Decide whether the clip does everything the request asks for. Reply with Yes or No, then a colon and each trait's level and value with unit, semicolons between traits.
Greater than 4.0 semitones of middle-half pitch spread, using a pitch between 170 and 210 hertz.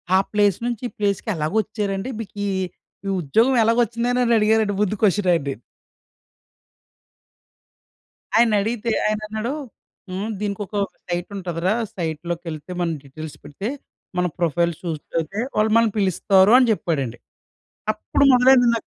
Yes: average, 4.4 semitones; high, 200 Hz